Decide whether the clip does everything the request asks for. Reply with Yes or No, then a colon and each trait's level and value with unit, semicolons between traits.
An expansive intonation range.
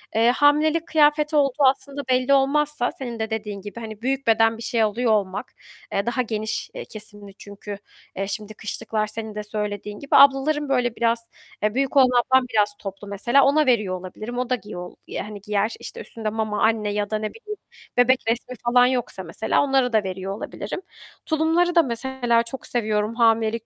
No: average, 4.1 semitones